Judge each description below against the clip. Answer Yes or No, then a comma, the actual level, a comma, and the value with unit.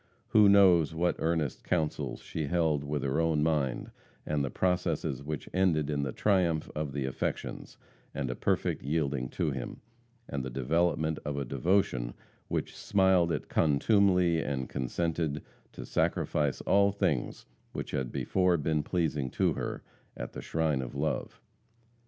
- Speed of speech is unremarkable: Yes, average, 150 wpm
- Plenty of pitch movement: No, average, 3.7 semitones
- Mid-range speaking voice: No, very low, 80 Hz